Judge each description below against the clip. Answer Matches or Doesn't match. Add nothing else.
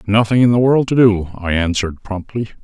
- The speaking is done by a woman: Doesn't match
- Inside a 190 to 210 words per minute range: Matches